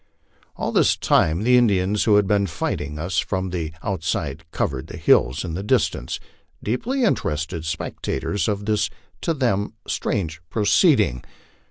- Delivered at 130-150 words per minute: Yes, average, 145 wpm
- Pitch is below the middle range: Yes, very low, 95 Hz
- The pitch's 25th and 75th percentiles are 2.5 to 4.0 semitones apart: No, average, 4.8 semitones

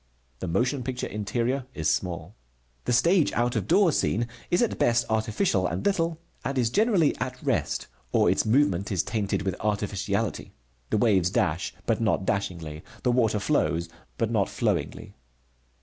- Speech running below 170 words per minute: Yes, average, 160 wpm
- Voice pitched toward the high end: No, low, 110 Hz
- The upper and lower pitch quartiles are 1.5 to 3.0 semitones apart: No, average, 4.7 semitones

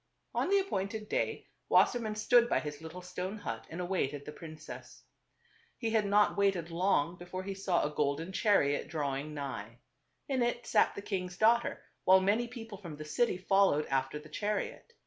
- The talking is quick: No, average, 180 wpm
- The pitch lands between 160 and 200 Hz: Yes, medium, 185 Hz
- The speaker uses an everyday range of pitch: No, wide, 5.7 semitones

